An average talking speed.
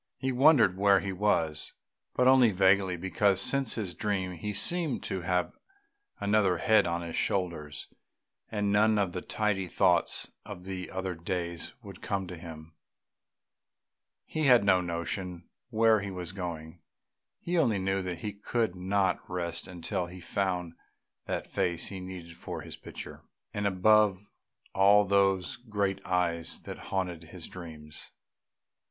Yes: average, 145 wpm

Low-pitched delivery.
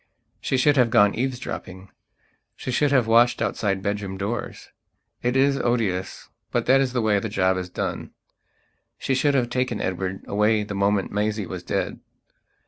Yes: low, 110 Hz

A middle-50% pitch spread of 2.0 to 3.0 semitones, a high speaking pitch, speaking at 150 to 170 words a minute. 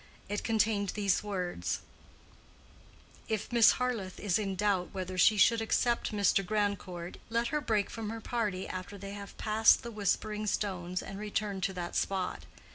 Yes: narrow, 2.6 semitones; high, 205 Hz; average, 160 wpm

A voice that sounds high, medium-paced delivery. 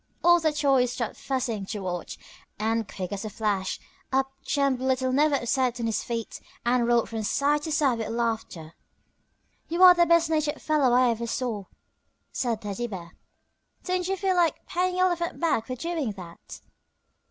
Yes: very high, 255 Hz; average, 175 wpm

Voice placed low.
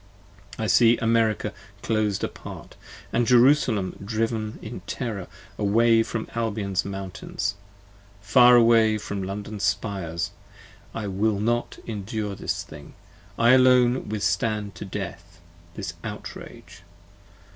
Yes: low, 110 Hz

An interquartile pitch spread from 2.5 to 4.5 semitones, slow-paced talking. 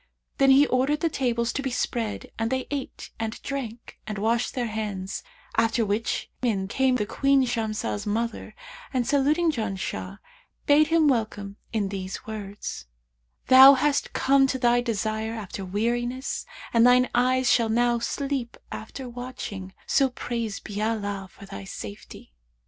No: average, 3.6 semitones; average, 150 wpm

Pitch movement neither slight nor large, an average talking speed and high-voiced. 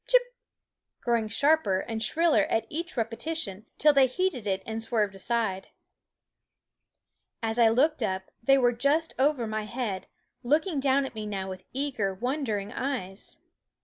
Yes: average, 5.0 semitones; average, 145 wpm; high, 235 Hz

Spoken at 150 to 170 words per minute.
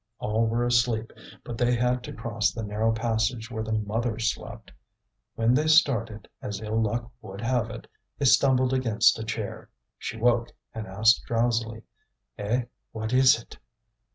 Yes: average, 160 wpm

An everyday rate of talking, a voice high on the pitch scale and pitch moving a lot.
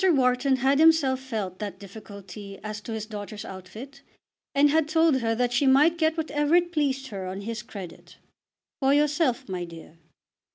Yes: average, 170 wpm; very high, 250 Hz; wide, 6.2 semitones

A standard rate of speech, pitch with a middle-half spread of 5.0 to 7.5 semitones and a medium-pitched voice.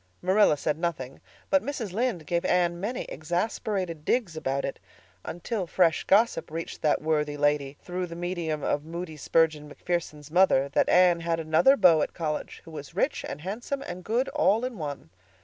No: average, 175 wpm; average, 3.8 semitones; medium, 170 Hz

